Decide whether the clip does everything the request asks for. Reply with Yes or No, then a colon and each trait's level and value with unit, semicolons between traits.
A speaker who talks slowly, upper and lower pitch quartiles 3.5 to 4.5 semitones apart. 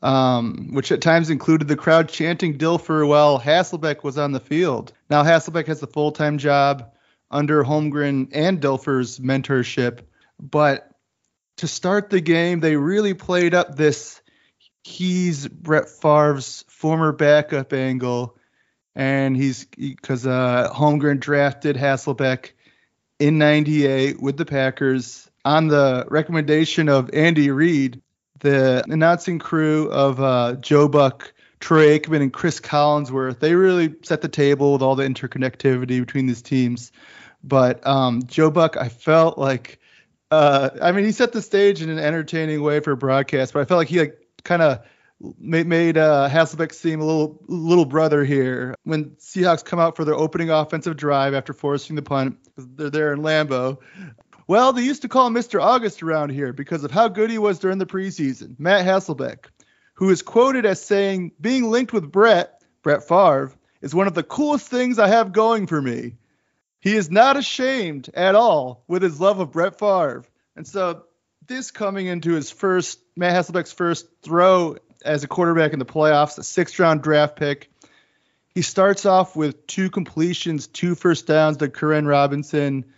No: average, 165 wpm; average, 4.0 semitones